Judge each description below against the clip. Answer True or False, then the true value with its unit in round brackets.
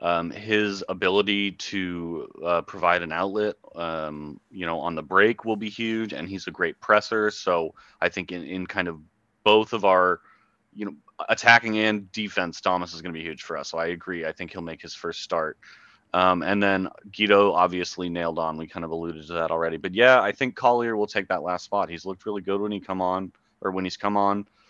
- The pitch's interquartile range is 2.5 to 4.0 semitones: True (3.5 semitones)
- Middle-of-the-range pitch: False (95 Hz)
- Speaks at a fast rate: True (225 wpm)